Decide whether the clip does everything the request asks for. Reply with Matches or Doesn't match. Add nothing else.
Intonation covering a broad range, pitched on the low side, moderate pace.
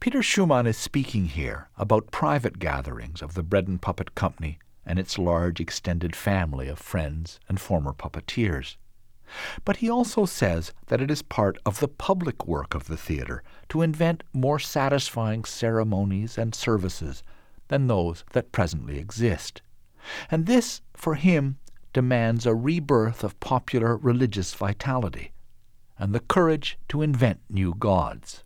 Matches